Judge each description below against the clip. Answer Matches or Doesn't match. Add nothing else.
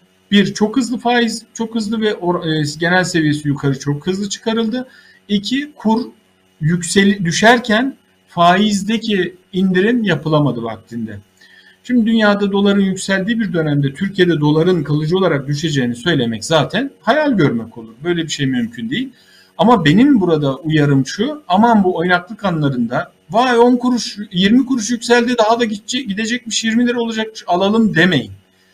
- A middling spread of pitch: Doesn't match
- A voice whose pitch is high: Matches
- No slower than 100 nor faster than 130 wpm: Doesn't match